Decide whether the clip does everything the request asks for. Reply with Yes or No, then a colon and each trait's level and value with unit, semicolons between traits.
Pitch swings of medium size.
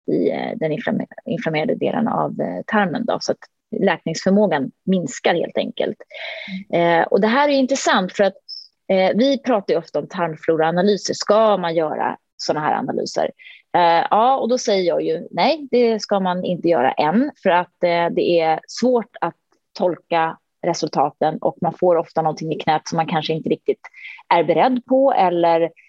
No: wide, 6.8 semitones